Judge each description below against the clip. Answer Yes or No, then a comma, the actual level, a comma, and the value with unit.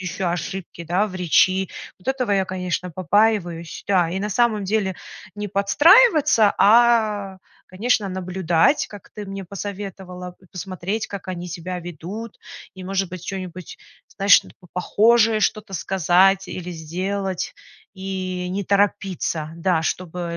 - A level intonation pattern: Yes, narrow, 2.3 semitones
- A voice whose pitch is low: No, high, 190 Hz